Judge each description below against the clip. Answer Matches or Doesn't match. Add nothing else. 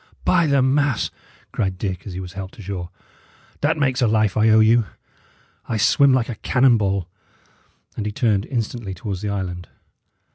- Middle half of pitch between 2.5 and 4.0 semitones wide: Doesn't match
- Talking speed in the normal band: Matches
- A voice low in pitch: Matches